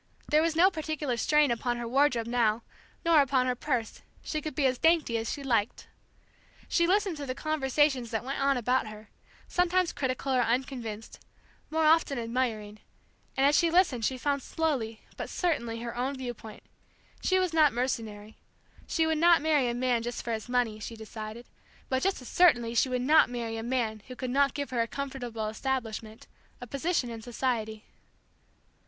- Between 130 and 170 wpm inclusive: No, average, 185 wpm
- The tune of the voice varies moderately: Yes, average, 4.4 semitones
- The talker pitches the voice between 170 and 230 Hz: No, very high, 255 Hz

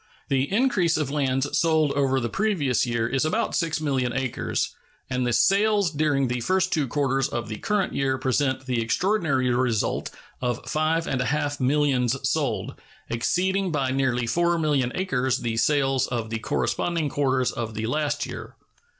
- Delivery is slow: No, average, 160 wpm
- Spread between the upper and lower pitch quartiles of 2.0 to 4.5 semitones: Yes, average, 3.9 semitones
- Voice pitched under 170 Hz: Yes, low, 135 Hz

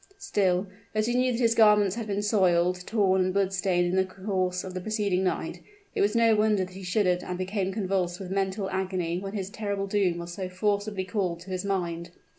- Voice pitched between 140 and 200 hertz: Yes, high, 190 Hz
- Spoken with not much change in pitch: Yes, narrow, 2.2 semitones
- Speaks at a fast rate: Yes, fast, 220 wpm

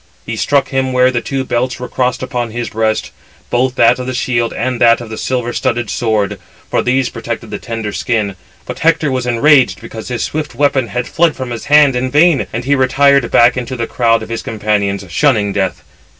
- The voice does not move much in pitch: Yes, narrow, 2.3 semitones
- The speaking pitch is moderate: No, low, 120 Hz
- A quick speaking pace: Yes, fast, 210 wpm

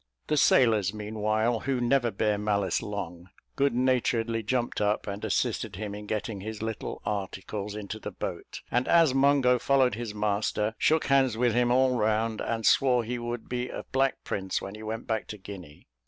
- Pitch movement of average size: Yes, average, 3.0 semitones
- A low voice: Yes, low, 110 Hz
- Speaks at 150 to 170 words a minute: No, average, 185 wpm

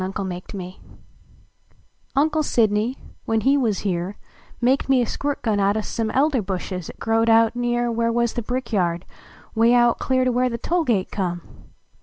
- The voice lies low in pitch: No, high, 230 Hz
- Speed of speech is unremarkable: Yes, average, 185 wpm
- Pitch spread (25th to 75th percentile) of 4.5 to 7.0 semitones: No, average, 3.8 semitones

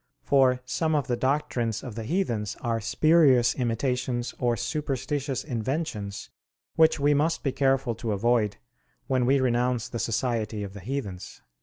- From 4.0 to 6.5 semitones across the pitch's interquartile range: No, average, 3.3 semitones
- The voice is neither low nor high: No, low, 125 Hz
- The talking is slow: No, average, 150 wpm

